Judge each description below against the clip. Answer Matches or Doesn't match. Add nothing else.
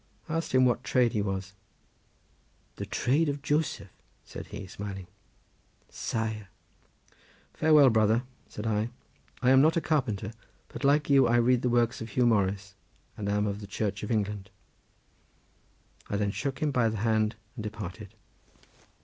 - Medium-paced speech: Matches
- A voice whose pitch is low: Matches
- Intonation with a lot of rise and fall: Doesn't match